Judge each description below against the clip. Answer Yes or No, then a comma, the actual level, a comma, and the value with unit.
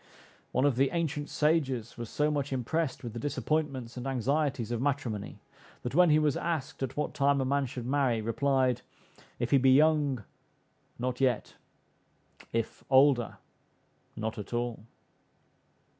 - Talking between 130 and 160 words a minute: Yes, average, 150 wpm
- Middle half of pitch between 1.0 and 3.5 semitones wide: Yes, average, 3.2 semitones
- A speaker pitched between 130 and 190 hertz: Yes, low, 135 Hz